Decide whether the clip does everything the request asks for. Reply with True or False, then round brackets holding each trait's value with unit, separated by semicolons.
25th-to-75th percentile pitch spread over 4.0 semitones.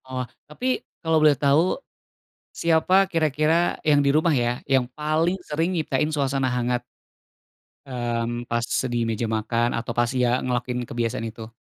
True (4.4 semitones)